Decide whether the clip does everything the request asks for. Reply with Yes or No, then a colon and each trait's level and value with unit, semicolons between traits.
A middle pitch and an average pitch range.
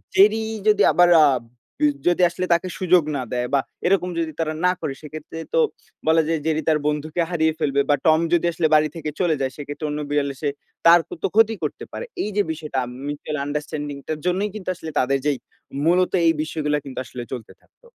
Yes: medium, 155 Hz; average, 3.2 semitones